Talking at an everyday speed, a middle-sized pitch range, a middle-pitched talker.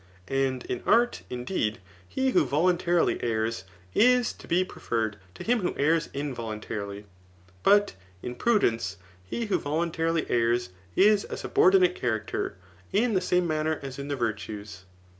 No: average, 145 wpm; wide, 8.3 semitones; medium, 145 Hz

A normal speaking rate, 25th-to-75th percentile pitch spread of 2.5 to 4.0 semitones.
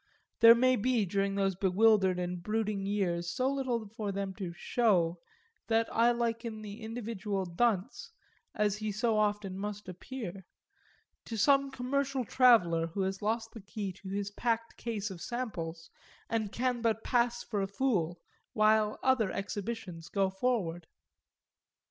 Yes: average, 150 wpm; average, 3.3 semitones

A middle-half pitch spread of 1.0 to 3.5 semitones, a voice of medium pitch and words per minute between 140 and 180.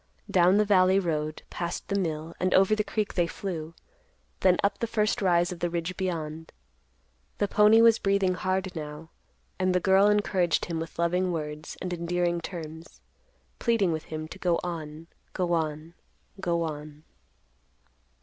Yes: average, 2.8 semitones; medium, 175 Hz; average, 160 wpm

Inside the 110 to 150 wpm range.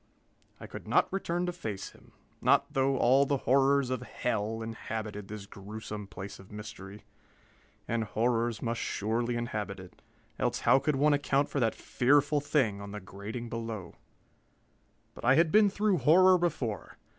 No: average, 160 wpm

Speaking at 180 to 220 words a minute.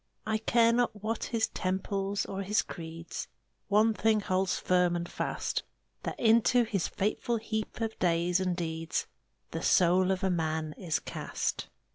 No: average, 155 wpm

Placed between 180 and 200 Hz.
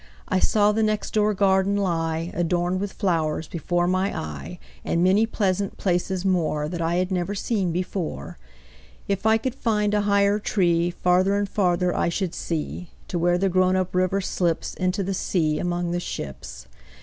Yes: medium, 185 Hz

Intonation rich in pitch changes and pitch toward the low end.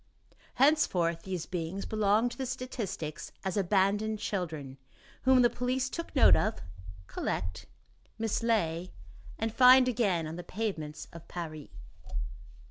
No: wide, 6.3 semitones; high, 200 Hz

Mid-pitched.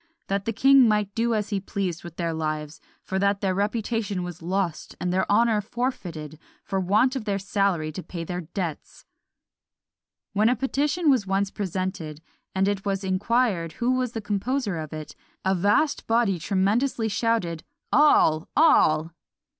No: high, 200 Hz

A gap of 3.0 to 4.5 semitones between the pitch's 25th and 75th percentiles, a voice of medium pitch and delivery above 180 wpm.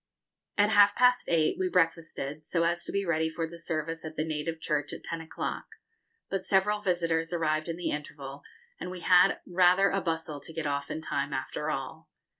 No: narrow, 2.6 semitones; medium, 165 Hz; average, 200 wpm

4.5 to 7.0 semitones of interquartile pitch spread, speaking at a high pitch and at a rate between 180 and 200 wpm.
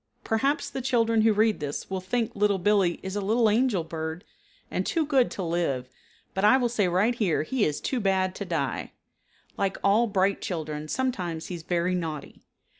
Yes: average, 4.9 semitones; high, 195 Hz; average, 190 wpm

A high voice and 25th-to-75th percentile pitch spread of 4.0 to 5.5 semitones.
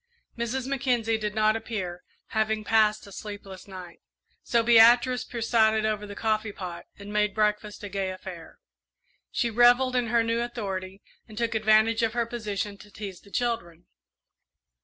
No: high, 215 Hz; narrow, 2.4 semitones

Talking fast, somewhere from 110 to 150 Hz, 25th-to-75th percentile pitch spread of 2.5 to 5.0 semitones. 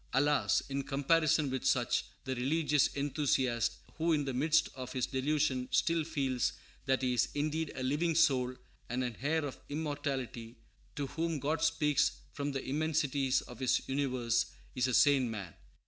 No: average, 165 wpm; medium, 140 Hz; average, 2.9 semitones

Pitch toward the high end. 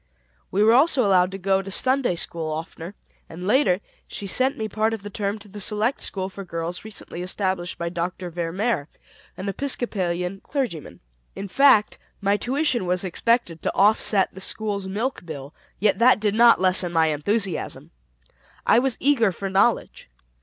Yes: high, 195 Hz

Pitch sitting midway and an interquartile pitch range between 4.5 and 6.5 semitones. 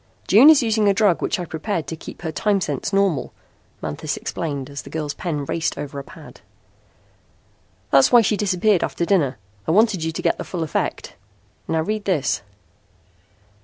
Yes: medium, 170 Hz; wide, 5.5 semitones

